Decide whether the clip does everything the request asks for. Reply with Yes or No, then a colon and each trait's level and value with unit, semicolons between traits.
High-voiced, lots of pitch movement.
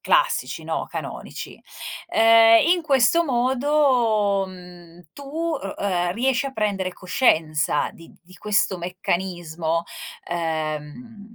Yes: high, 205 Hz; wide, 6.6 semitones